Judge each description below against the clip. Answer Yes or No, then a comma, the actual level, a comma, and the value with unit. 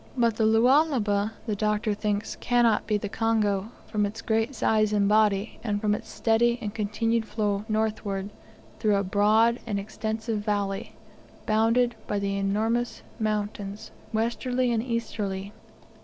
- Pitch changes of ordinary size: No, narrow, 1.7 semitones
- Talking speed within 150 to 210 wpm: No, average, 140 wpm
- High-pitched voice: Yes, high, 215 Hz